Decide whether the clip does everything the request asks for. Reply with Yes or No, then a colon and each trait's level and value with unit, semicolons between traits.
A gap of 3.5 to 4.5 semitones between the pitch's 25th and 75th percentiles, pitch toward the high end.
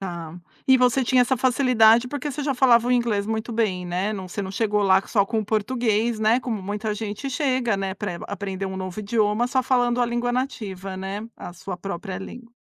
Yes: average, 4.0 semitones; high, 220 Hz